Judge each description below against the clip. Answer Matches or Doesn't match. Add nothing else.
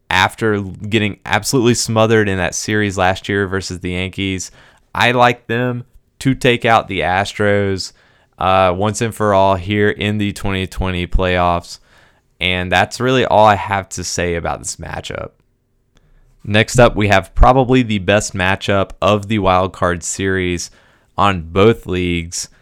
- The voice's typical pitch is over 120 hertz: Doesn't match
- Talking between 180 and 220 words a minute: Doesn't match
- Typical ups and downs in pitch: Matches